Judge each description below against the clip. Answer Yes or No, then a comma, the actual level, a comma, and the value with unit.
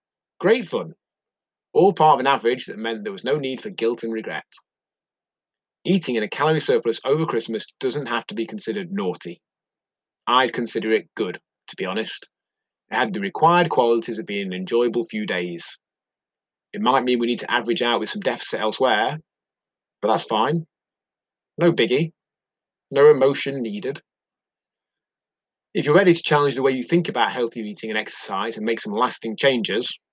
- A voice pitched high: No, low, 120 Hz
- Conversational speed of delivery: Yes, average, 175 wpm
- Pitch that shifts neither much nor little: No, wide, 6.0 semitones